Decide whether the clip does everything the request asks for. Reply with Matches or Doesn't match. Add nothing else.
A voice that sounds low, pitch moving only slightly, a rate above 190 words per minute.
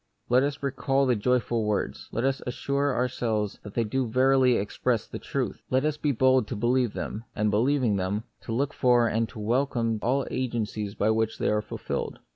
Doesn't match